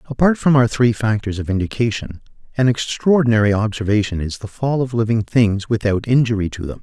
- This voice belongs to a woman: No, male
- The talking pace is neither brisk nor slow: Yes, average, 175 wpm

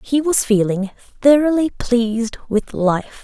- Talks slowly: Yes, slow, 130 wpm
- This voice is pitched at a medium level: No, high, 240 Hz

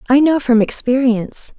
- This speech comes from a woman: Yes, female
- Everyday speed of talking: Yes, average, 150 wpm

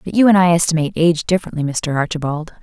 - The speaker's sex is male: No, female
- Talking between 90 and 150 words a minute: No, fast, 205 wpm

